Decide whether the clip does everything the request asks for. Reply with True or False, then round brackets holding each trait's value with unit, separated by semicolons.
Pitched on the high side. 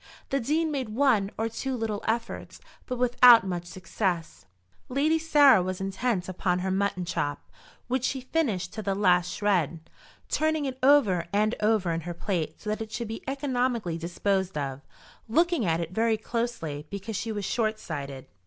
True (215 Hz)